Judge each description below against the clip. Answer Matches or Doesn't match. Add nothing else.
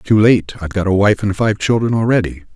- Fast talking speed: Matches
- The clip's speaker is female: Doesn't match